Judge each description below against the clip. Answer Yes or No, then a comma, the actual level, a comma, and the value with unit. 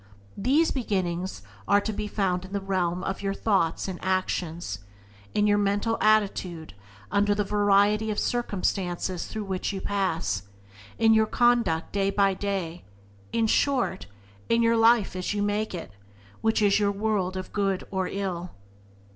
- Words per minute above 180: No, average, 165 wpm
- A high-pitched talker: Yes, high, 200 Hz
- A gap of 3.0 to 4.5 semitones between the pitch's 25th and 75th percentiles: No, narrow, 2.5 semitones